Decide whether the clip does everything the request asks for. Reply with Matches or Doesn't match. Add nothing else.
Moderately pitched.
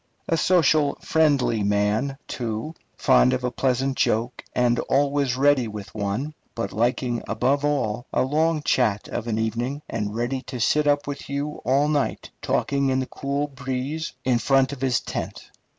Doesn't match